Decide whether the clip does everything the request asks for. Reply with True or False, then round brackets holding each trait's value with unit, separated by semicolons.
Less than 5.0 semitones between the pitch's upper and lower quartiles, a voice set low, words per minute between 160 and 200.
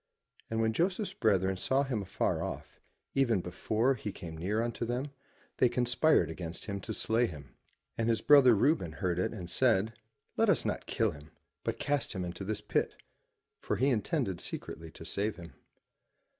False (5.3 semitones; 110 Hz; 175 wpm)